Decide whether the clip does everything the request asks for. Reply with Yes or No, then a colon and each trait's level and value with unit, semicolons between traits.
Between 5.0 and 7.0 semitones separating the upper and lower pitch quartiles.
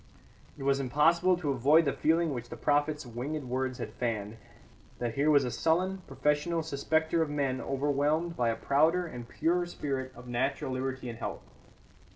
No: average, 3.7 semitones